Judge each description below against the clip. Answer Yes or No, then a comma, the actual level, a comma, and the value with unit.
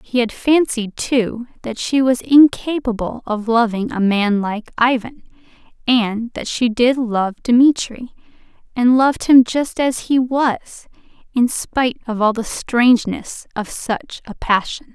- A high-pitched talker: Yes, high, 240 Hz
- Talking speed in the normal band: Yes, average, 150 wpm